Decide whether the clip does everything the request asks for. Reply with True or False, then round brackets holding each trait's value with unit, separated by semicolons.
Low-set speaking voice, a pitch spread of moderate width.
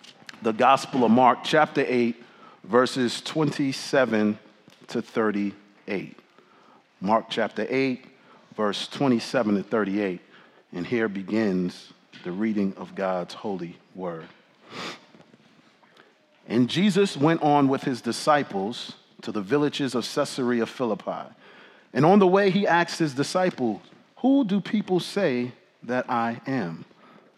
False (125 Hz; 6.2 semitones)